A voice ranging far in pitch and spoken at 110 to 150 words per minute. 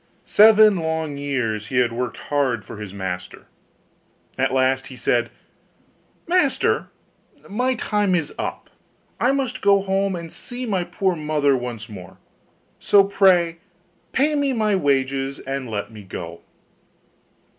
Yes: wide, 8.7 semitones; slow, 135 wpm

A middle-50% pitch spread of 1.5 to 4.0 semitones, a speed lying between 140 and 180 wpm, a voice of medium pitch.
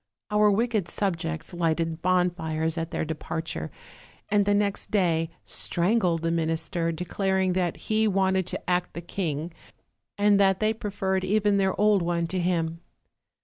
Yes: average, 3.2 semitones; average, 155 wpm; medium, 180 Hz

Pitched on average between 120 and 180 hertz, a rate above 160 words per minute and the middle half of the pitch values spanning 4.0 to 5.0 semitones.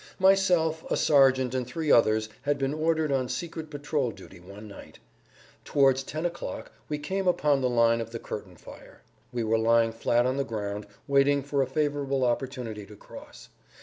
Yes: low, 135 Hz; average, 180 wpm; average, 4.4 semitones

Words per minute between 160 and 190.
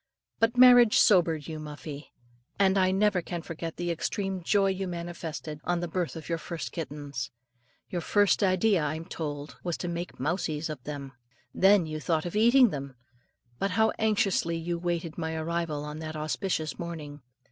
Yes: average, 170 wpm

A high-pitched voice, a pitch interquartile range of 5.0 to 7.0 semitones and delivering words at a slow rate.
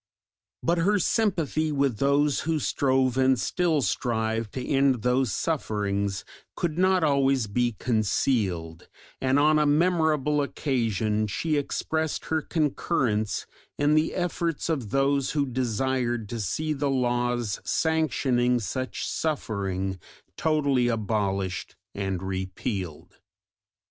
No: low, 130 Hz; wide, 5.6 semitones; slow, 115 wpm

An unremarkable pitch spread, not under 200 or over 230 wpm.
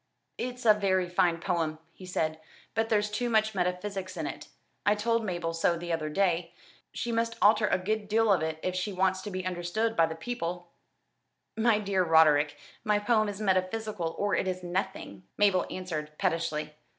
No: average, 3.9 semitones; average, 185 wpm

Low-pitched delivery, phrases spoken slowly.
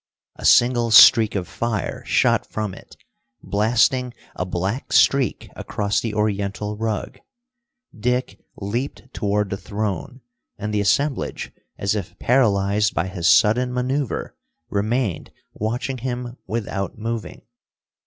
Yes: low, 110 Hz; slow, 120 wpm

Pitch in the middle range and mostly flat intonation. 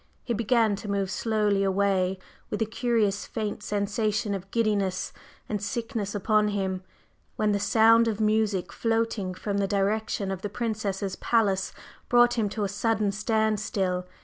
No: high, 210 Hz; narrow, 2.1 semitones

